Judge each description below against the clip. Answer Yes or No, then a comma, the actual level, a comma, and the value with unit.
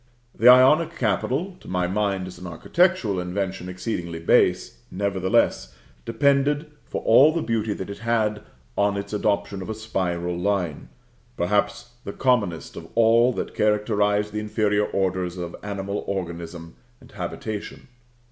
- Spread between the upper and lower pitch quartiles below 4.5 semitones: Yes, average, 3.7 semitones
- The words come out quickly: No, average, 140 wpm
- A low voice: Yes, low, 100 Hz